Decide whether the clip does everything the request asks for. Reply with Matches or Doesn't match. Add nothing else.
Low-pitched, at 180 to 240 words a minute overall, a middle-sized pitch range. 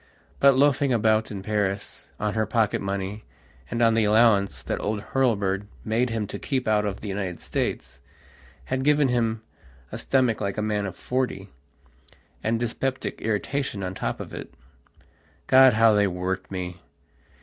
Doesn't match